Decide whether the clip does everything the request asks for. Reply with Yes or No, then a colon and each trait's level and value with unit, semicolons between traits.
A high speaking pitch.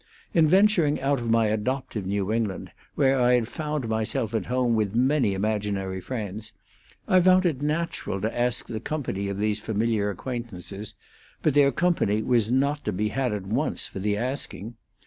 No: low, 115 Hz